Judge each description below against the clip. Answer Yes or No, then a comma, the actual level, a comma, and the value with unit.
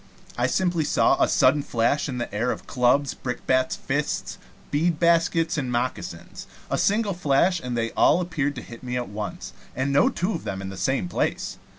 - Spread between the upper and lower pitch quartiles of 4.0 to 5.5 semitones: Yes, average, 5.1 semitones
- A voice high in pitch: No, low, 135 Hz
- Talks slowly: No, average, 195 wpm